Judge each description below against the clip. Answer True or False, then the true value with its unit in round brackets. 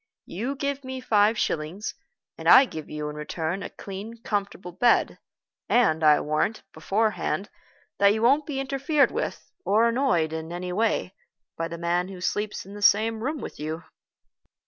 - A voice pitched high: True (205 Hz)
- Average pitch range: False (6.1 semitones)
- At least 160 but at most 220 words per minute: True (165 wpm)